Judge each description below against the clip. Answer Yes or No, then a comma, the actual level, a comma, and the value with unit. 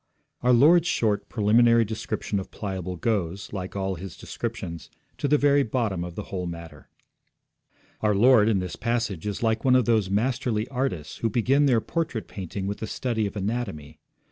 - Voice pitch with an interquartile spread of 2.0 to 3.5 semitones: No, average, 4.1 semitones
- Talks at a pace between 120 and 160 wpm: No, average, 175 wpm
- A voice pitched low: Yes, low, 110 Hz